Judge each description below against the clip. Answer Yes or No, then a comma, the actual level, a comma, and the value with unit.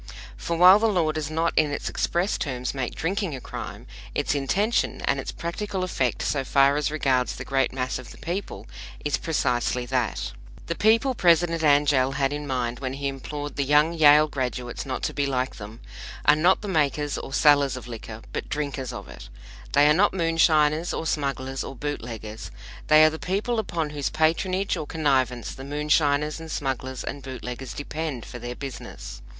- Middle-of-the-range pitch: Yes, medium, 145 Hz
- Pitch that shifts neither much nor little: Yes, average, 3.7 semitones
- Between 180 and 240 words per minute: Yes, average, 185 wpm